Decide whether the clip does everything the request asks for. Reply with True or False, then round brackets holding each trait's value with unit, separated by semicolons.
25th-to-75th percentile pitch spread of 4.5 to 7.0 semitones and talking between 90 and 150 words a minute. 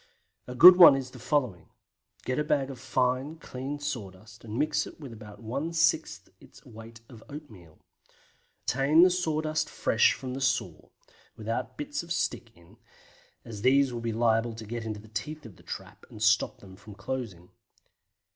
False (4.9 semitones; 185 wpm)